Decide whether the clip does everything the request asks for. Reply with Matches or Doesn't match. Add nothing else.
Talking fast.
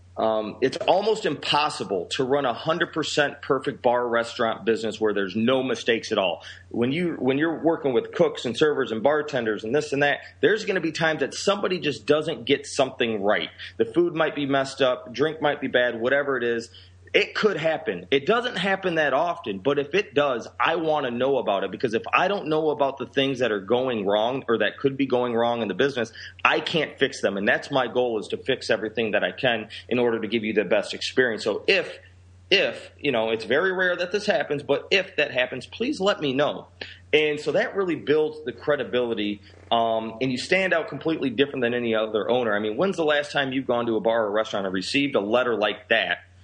Matches